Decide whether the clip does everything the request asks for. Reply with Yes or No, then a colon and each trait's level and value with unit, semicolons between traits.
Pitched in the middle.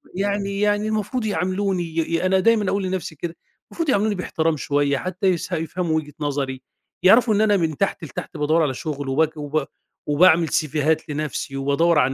Yes: medium, 165 Hz